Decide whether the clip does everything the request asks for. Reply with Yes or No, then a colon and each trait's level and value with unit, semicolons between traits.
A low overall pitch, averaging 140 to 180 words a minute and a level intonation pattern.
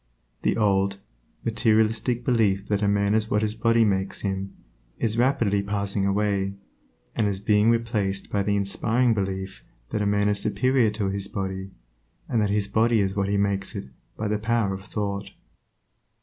Yes: low, 105 Hz; average, 170 wpm; narrow, 1.9 semitones